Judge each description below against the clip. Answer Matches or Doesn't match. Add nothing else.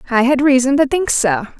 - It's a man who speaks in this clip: Doesn't match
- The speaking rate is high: Matches